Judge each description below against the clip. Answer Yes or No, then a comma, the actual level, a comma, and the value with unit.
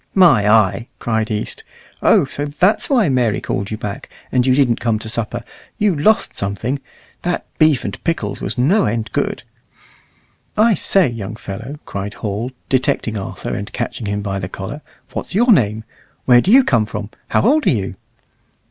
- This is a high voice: No, low, 120 Hz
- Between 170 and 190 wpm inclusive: Yes, average, 175 wpm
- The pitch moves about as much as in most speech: No, wide, 6.4 semitones